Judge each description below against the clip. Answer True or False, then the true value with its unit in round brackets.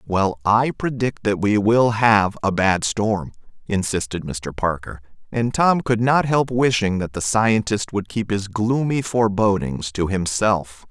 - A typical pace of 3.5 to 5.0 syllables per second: True (4.0 syllables/s)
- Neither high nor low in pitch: False (105 Hz)